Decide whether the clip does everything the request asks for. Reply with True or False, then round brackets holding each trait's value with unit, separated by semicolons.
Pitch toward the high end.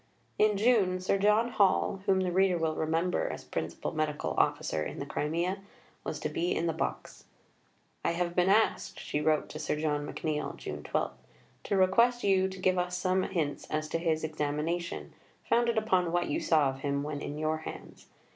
False (170 Hz)